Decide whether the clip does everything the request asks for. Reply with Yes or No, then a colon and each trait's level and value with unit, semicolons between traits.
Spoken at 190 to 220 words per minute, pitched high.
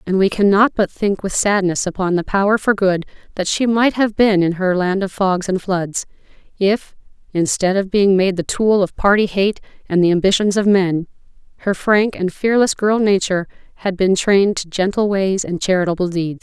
Yes: average, 195 wpm; high, 195 Hz